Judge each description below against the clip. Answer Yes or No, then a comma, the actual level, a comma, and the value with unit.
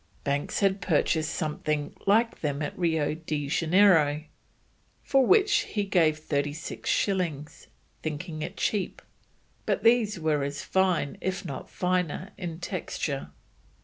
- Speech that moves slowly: Yes, slow, 130 wpm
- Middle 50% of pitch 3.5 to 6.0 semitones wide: Yes, average, 4.2 semitones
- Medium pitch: Yes, medium, 165 Hz